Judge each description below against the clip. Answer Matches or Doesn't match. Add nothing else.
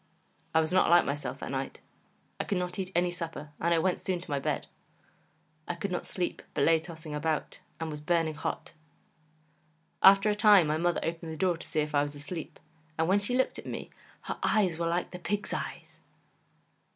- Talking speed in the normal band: Doesn't match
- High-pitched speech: Doesn't match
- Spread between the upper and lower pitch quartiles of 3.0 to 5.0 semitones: Doesn't match